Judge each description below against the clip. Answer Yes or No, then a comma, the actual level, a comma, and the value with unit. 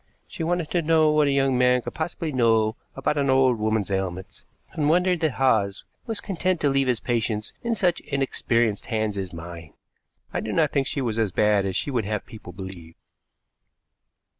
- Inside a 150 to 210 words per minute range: Yes, average, 190 wpm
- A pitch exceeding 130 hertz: No, low, 125 Hz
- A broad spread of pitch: Yes, wide, 6.4 semitones